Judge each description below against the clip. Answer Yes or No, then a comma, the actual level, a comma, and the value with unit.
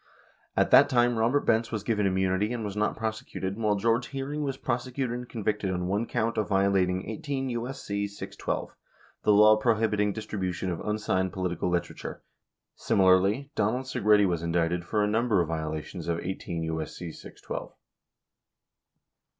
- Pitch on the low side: Yes, low, 105 Hz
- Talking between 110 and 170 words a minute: Yes, average, 150 wpm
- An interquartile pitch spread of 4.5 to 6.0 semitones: No, average, 3.8 semitones